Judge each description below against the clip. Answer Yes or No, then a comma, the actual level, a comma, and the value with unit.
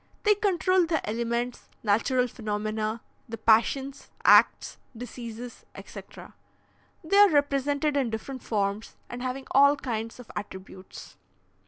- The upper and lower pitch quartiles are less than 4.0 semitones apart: No, average, 4.3 semitones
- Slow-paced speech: Yes, slow, 120 wpm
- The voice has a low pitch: No, high, 245 Hz